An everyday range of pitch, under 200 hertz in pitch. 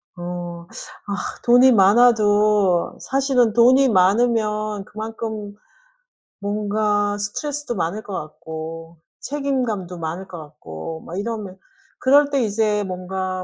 No: average, 4.2 semitones; high, 205 Hz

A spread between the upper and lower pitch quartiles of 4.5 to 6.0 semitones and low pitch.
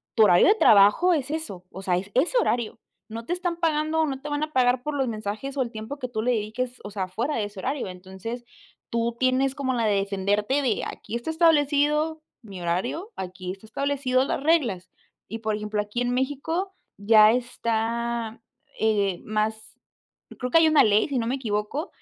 No: average, 5.3 semitones; high, 235 Hz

